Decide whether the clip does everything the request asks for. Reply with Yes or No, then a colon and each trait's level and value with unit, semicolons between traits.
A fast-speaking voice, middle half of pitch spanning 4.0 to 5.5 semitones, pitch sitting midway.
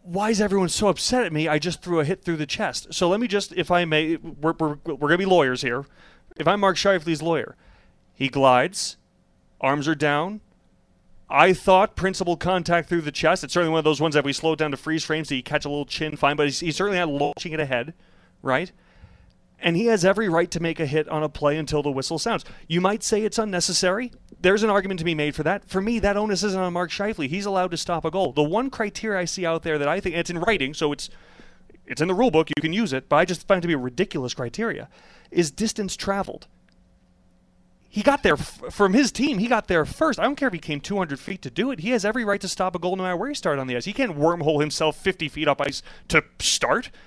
Yes: fast, 260 wpm; average, 4.7 semitones; medium, 170 Hz